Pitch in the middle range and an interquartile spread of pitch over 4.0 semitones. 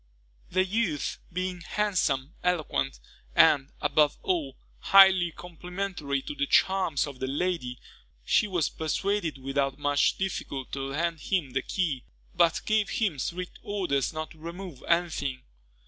Yes: medium, 165 Hz; average, 4.7 semitones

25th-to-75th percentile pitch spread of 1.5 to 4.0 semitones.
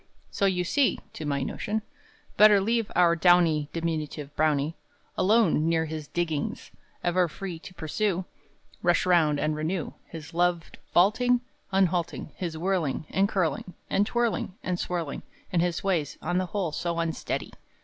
Yes: average, 3.3 semitones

